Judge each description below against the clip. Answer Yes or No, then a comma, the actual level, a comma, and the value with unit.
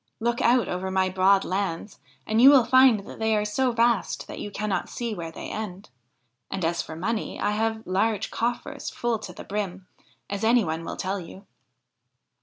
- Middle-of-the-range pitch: No, high, 210 Hz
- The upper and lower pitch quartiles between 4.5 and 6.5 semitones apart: No, average, 3.3 semitones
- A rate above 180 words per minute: Yes, average, 195 wpm